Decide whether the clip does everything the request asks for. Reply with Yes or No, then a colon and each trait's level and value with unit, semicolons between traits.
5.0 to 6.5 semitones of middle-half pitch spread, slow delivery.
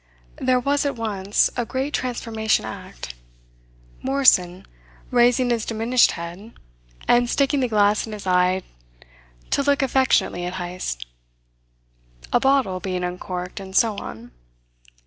Yes: wide, 5.6 semitones; slow, 125 wpm